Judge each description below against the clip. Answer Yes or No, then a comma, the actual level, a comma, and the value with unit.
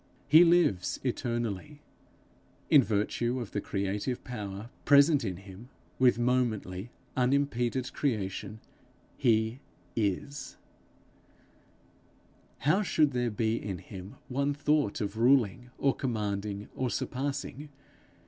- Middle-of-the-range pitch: No, low, 120 Hz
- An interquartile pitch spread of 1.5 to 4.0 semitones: No, average, 5.0 semitones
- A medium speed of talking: No, slow, 105 wpm